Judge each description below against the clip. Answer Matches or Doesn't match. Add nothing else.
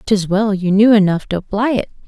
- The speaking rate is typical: Doesn't match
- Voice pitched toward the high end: Matches